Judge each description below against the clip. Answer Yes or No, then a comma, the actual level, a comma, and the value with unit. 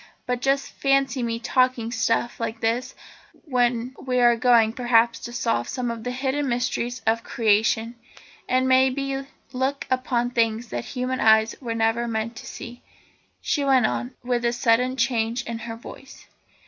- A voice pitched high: Yes, high, 240 Hz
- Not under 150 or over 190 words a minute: Yes, average, 165 wpm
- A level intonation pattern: Yes, narrow, 2.1 semitones